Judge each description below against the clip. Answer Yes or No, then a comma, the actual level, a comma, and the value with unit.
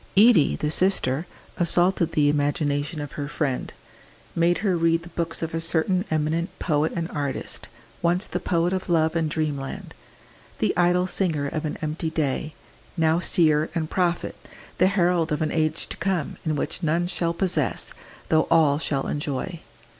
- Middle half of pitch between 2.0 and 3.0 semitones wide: Yes, narrow, 2.5 semitones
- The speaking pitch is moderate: Yes, medium, 160 Hz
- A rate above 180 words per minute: No, average, 165 wpm